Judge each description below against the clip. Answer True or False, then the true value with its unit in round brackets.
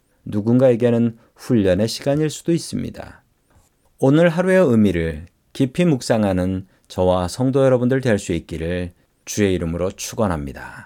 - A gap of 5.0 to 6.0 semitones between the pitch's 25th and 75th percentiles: False (6.6 semitones)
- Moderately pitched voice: False (110 Hz)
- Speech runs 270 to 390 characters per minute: True (310 characters per minute)